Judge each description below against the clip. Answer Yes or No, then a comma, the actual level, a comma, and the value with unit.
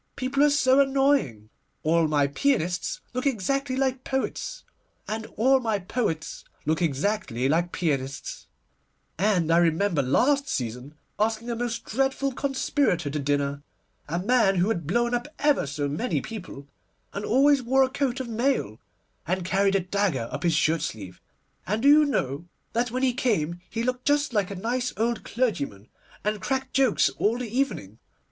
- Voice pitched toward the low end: No, high, 215 Hz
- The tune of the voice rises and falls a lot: Yes, wide, 8.4 semitones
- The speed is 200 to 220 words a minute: No, average, 165 wpm